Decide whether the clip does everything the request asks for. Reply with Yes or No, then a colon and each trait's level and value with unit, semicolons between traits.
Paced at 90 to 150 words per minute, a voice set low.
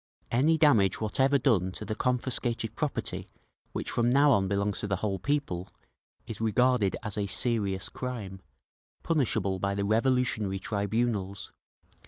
Yes: average, 140 wpm; low, 110 Hz